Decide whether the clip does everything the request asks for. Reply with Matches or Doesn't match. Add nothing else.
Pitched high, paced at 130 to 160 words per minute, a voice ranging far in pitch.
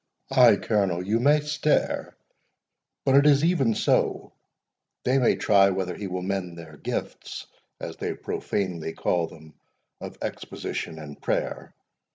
Doesn't match